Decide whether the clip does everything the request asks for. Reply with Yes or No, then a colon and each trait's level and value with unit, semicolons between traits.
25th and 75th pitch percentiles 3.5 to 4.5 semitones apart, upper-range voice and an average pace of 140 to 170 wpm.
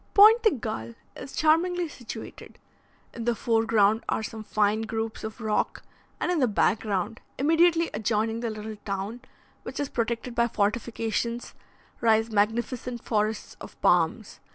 No: narrow, 2.5 semitones; high, 225 Hz; average, 150 wpm